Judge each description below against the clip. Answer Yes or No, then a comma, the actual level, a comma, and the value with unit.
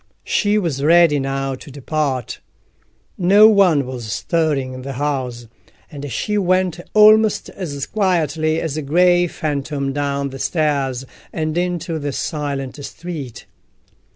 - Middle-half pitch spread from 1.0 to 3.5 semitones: No, average, 4.3 semitones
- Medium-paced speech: No, slow, 130 wpm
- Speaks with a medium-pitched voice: Yes, medium, 150 Hz